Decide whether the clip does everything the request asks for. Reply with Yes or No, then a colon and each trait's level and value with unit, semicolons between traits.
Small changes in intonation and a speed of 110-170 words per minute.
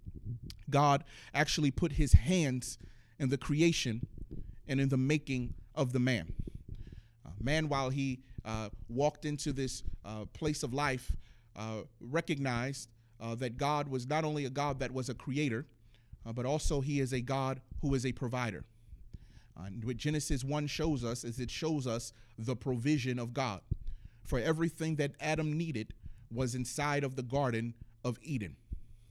No: average, 4.2 semitones; average, 165 wpm